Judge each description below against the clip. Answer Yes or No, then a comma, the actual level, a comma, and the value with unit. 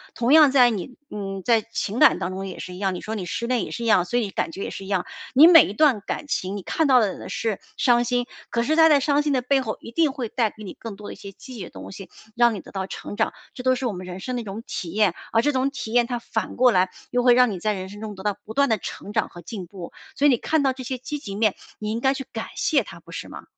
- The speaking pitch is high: Yes, high, 230 Hz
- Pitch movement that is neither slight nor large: Yes, average, 4.7 semitones